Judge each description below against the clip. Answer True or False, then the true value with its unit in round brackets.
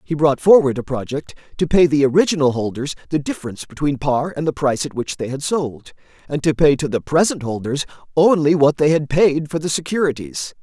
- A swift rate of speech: True (210 wpm)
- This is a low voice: False (150 Hz)